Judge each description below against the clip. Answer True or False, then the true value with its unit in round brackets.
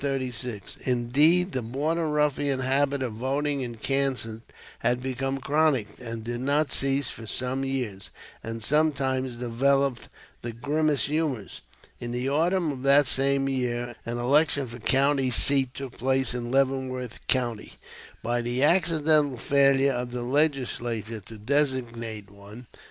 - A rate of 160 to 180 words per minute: False (135 wpm)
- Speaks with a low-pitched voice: True (130 Hz)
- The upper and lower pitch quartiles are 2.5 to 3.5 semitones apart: True (2.8 semitones)